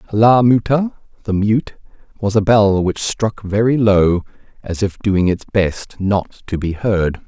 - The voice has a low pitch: Yes, low, 105 Hz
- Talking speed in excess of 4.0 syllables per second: No, 3.9 syllables/s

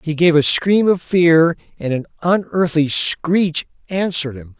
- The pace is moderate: Yes, average, 155 wpm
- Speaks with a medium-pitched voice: Yes, medium, 165 Hz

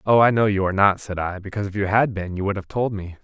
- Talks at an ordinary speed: No, fast, 335 wpm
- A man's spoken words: Yes, male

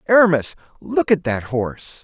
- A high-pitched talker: No, medium, 145 Hz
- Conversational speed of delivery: Yes, average, 145 wpm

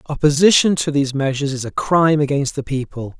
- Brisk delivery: No, average, 190 wpm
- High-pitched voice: No, medium, 145 Hz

